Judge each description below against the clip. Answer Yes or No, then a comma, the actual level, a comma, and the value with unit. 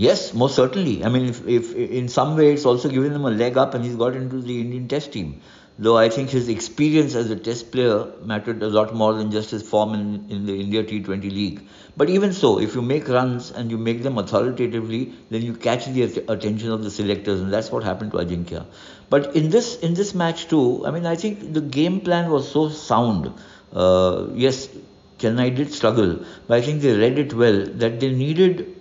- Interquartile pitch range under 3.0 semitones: No, average, 4.7 semitones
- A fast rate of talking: Yes, fast, 225 wpm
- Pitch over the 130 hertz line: No, low, 120 Hz